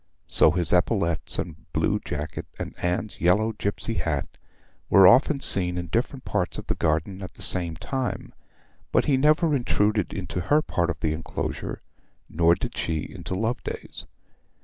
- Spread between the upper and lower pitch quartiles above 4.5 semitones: Yes, average, 5.1 semitones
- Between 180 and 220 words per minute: No, average, 160 wpm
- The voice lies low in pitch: Yes, very low, 95 Hz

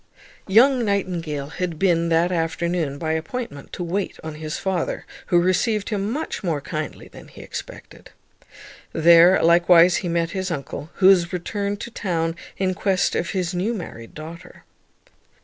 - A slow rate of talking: No, average, 155 wpm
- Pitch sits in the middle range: Yes, medium, 175 Hz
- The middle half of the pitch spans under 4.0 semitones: Yes, average, 2.9 semitones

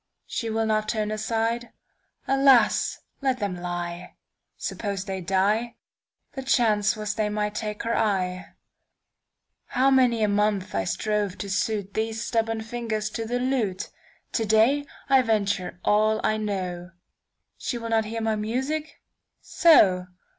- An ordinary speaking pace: No, slow, 125 wpm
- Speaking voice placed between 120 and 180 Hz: No, high, 215 Hz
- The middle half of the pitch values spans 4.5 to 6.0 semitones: No, narrow, 2.4 semitones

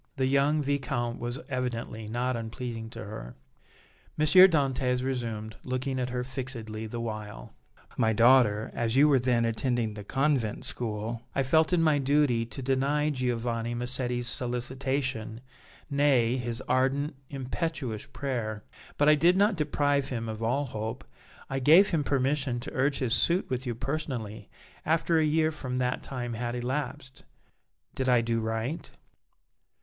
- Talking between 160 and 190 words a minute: No, average, 150 wpm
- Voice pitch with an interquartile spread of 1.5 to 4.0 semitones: Yes, average, 3.4 semitones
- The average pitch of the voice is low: Yes, low, 125 Hz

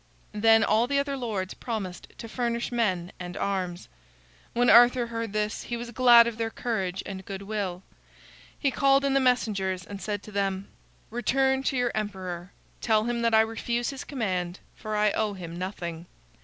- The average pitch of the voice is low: No, high, 220 Hz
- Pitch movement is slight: No, average, 3.9 semitones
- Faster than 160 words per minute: Yes, average, 180 wpm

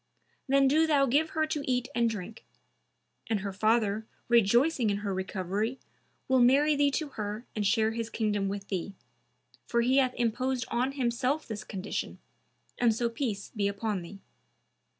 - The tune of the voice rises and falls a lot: No, average, 4.3 semitones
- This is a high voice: Yes, high, 230 Hz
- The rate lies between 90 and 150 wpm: No, average, 165 wpm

